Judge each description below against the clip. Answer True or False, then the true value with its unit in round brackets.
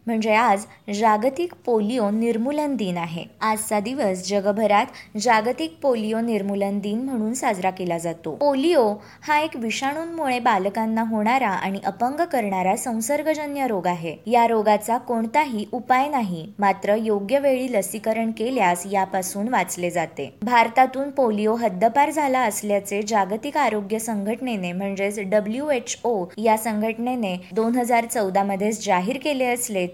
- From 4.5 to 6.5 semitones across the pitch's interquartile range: False (3.7 semitones)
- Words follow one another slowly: False (125 wpm)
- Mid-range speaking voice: False (220 Hz)